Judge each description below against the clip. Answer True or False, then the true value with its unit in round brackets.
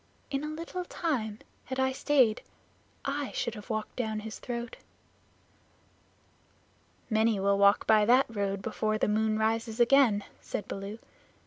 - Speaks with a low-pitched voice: False (220 Hz)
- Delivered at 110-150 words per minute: True (140 wpm)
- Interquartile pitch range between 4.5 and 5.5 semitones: False (3.5 semitones)